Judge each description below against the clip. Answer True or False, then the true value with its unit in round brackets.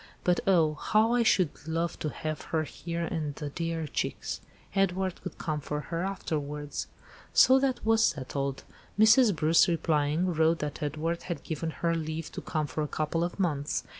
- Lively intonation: False (2.9 semitones)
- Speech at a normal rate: True (175 wpm)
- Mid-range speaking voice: True (165 Hz)